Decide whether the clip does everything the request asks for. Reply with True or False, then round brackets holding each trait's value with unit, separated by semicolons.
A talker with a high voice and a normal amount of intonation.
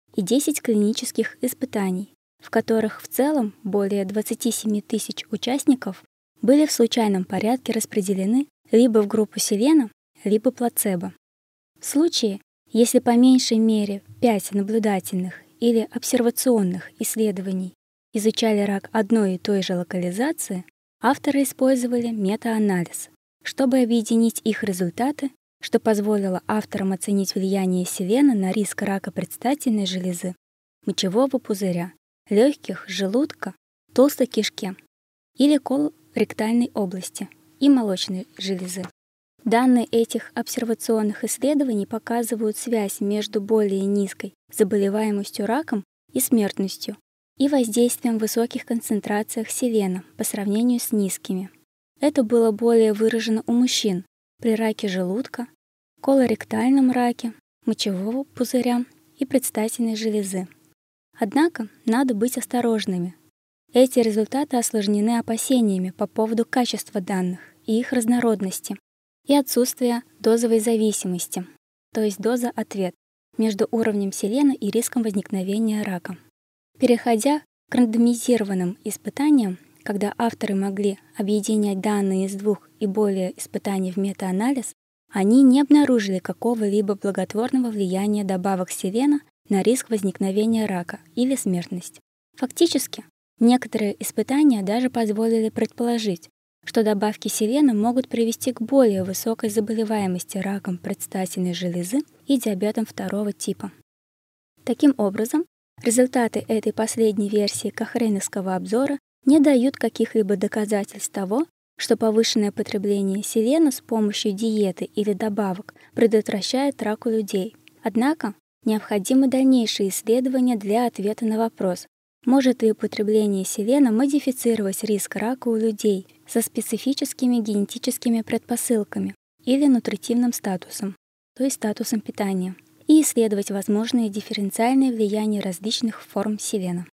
True (220 Hz; 3.1 semitones)